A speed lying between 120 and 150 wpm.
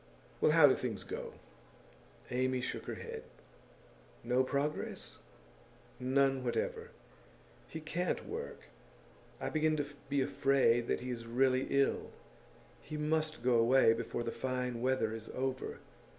Yes: slow, 135 wpm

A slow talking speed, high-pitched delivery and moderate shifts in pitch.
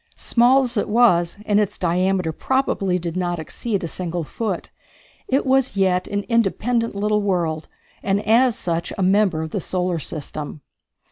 No: average, 160 wpm; high, 195 Hz; average, 4.8 semitones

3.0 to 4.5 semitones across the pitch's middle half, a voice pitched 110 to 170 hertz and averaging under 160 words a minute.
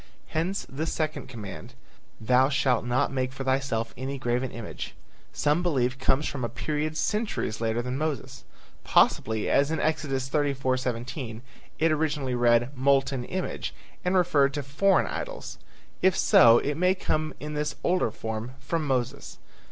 Yes: average, 3.8 semitones; low, 135 Hz; average, 150 wpm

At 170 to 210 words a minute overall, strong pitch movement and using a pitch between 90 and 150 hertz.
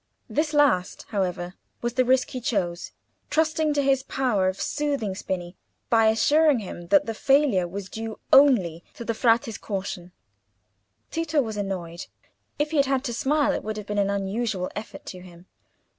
No: average, 175 wpm; wide, 6.3 semitones; high, 220 Hz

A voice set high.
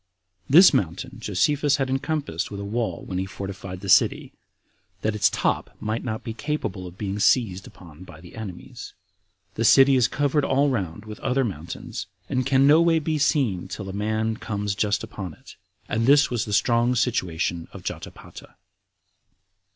No: low, 110 Hz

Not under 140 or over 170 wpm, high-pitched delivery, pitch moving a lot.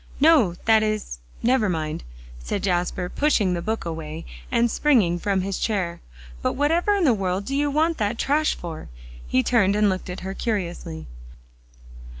Yes: average, 165 wpm; high, 200 Hz; wide, 6.2 semitones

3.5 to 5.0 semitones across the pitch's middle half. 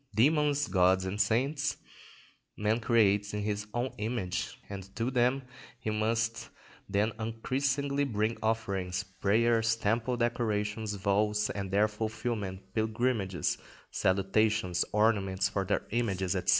No: average, 2.9 semitones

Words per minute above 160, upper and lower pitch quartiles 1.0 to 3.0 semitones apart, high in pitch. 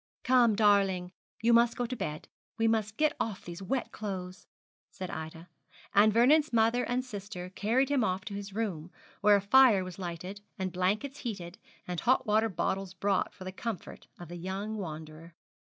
No: average, 180 wpm; average, 3.9 semitones; high, 200 Hz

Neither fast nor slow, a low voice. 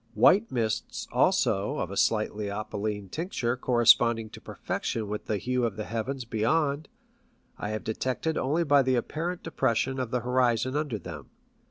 Yes: average, 160 wpm; low, 120 Hz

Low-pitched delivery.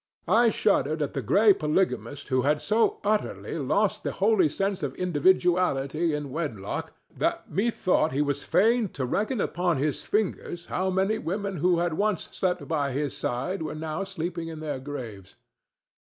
No: medium, 170 Hz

